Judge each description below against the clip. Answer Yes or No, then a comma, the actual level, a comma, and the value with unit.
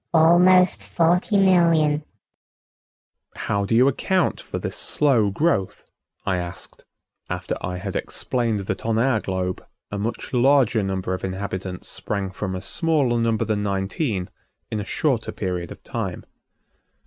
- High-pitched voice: No, low, 110 Hz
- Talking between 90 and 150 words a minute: Yes, average, 140 wpm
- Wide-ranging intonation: Yes, wide, 7.6 semitones